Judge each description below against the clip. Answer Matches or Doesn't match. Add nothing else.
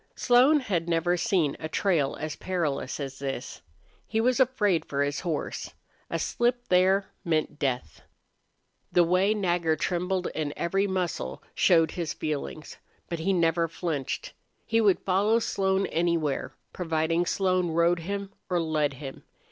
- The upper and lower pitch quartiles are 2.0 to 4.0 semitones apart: Matches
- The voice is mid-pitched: Matches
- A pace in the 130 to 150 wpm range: Matches